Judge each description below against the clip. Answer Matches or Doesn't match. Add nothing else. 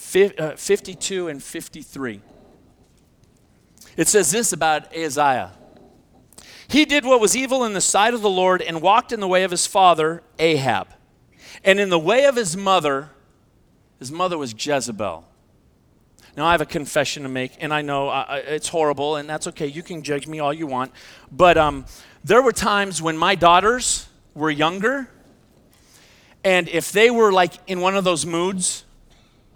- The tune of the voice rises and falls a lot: Doesn't match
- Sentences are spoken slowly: Doesn't match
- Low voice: Doesn't match